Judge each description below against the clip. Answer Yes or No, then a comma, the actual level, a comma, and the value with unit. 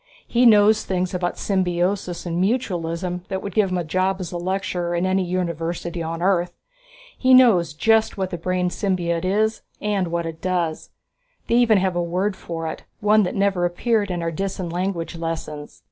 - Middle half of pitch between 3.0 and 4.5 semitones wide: No, narrow, 2.4 semitones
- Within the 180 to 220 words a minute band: Yes, average, 185 wpm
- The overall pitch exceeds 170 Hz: Yes, medium, 185 Hz